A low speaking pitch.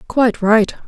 No: high, 225 Hz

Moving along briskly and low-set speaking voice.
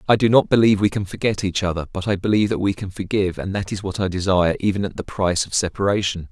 Yes: fast, 265 wpm; very low, 95 Hz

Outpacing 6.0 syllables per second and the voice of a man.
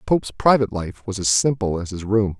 Yes: 6.5 syllables/s; male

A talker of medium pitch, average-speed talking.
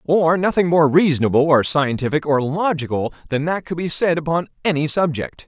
Yes: medium, 155 Hz; average, 175 wpm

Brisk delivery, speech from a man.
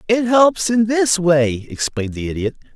No: average, 175 wpm; male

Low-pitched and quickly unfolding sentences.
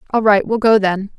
No: high, 210 Hz; fast, 255 wpm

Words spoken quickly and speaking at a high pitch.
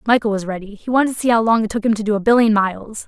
Yes: fast, 330 wpm; high, 220 Hz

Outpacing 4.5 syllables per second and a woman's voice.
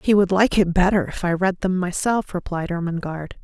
Yes: 5.4 syllables/s; female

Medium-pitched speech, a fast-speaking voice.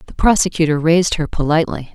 No: medium, 160 Hz; average, 155 wpm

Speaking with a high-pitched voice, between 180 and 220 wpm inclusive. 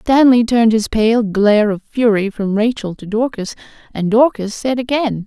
No: high, 225 Hz; average, 170 wpm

